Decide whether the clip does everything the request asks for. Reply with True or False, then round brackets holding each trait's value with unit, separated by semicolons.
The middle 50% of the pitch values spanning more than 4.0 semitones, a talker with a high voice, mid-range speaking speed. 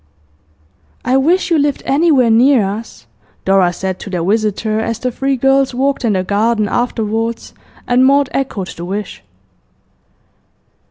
True (4.6 semitones; 230 Hz; 145 wpm)